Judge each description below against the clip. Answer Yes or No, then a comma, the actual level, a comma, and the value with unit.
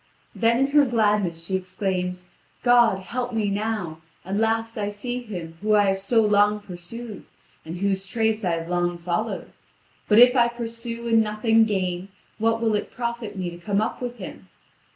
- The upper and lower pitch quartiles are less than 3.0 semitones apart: No, average, 3.6 semitones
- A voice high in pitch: Yes, high, 210 Hz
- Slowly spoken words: No, average, 180 wpm